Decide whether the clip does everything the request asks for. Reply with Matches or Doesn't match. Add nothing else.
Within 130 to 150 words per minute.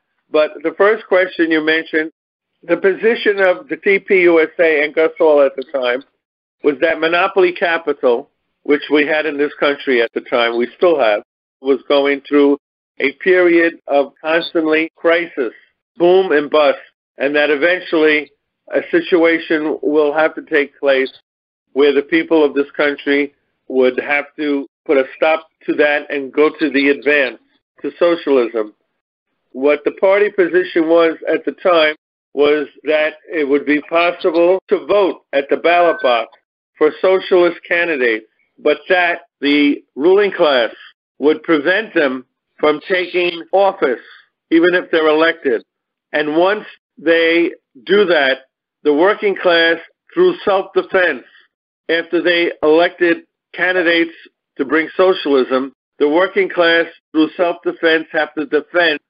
Matches